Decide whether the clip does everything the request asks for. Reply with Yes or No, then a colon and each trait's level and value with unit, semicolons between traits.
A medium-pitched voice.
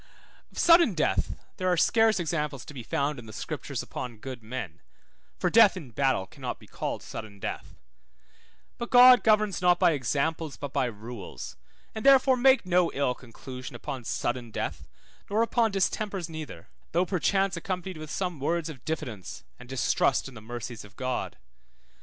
Yes: medium, 155 Hz